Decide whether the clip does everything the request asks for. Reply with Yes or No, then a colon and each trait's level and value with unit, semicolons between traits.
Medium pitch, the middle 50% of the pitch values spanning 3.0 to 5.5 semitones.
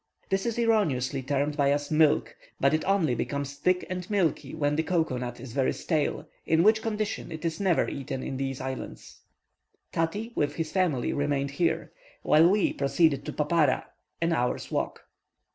Yes: medium, 155 Hz; average, 4.5 semitones